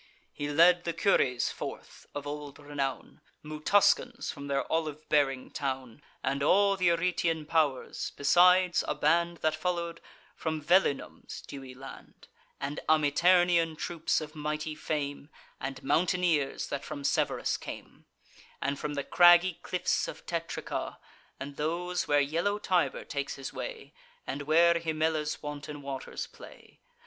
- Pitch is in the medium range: Yes, medium, 155 Hz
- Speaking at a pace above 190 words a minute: No, slow, 135 wpm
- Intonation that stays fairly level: No, average, 3.2 semitones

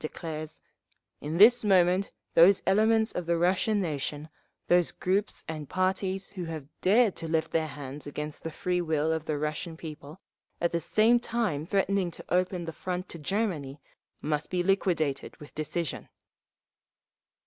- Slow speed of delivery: No, average, 155 wpm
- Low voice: No, medium, 170 Hz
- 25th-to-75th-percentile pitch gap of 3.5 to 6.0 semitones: Yes, average, 3.8 semitones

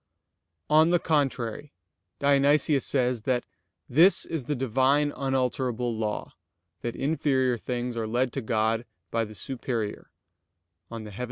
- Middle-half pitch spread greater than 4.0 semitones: No, average, 3.4 semitones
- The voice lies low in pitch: Yes, low, 130 Hz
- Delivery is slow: Yes, slow, 120 wpm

